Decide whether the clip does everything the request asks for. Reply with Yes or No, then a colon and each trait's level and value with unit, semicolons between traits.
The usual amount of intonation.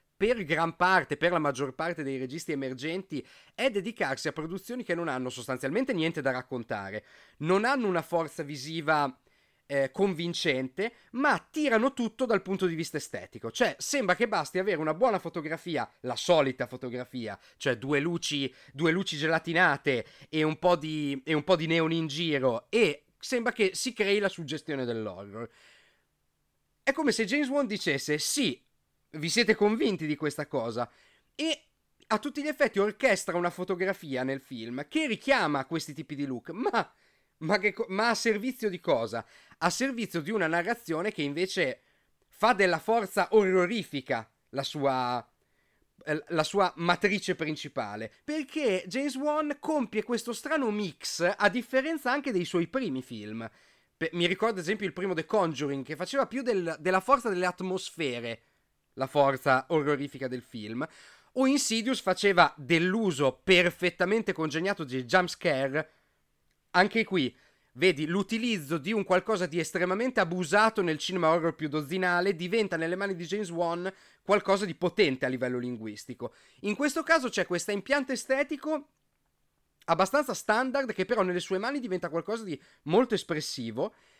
No: wide, 6.1 semitones